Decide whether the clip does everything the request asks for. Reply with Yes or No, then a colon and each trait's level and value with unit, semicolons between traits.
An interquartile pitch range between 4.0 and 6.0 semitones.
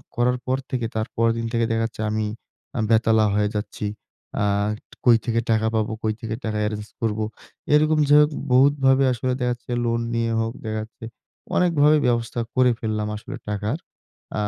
No: narrow, 2.4 semitones